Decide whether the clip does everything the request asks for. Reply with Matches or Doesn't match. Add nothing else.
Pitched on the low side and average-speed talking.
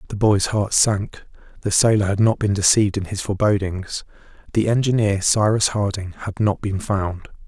Matches